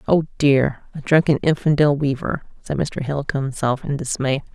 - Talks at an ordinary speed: Yes, average, 170 wpm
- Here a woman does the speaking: Yes, female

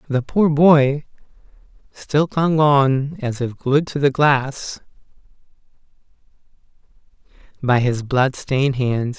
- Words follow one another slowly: Yes, slow, 110 wpm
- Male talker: Yes, male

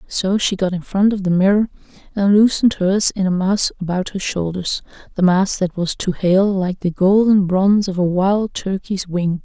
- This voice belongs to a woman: Yes, female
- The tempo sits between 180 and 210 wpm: Yes, average, 195 wpm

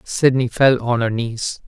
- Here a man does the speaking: Yes, male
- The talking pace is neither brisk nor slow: Yes, average, 180 wpm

